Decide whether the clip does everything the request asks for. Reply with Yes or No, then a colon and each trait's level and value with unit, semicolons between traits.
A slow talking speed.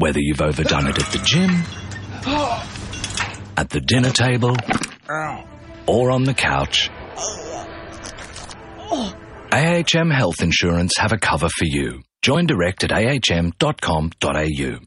Yes: slow, 110 wpm